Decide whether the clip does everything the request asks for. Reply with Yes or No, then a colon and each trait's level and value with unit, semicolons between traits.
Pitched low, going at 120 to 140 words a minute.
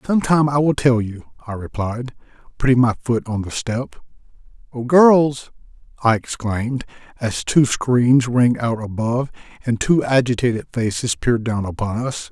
No: low, 120 Hz; average, 155 wpm